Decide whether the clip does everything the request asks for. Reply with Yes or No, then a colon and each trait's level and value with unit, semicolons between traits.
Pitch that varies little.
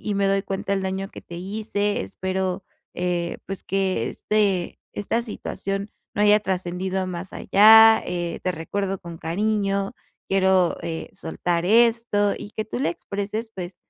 Yes: narrow, 2.3 semitones